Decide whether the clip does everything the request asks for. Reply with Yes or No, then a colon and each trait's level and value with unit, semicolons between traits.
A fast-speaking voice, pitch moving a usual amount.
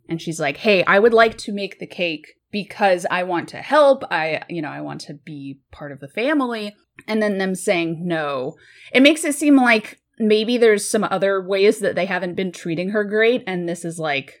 Yes: fast, 220 wpm; average, 5.0 semitones